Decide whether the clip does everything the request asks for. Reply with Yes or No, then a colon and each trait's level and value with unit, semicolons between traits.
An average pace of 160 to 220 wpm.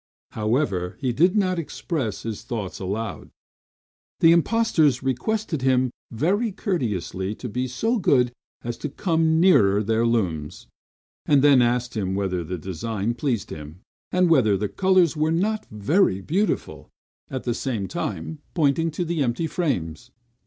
No: average, 145 wpm